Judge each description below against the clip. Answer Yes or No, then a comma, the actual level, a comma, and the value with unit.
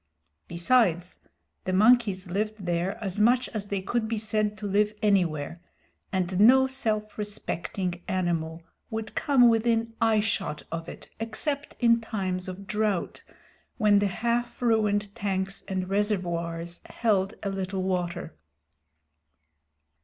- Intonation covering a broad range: No, average, 3.2 semitones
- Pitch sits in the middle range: No, high, 205 Hz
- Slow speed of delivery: Yes, slow, 125 wpm